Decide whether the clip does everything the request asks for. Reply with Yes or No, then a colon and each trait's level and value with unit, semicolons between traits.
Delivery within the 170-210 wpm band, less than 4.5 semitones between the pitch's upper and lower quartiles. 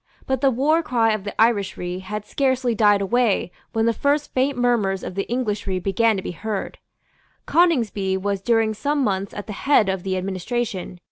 Yes: average, 185 wpm; average, 4.1 semitones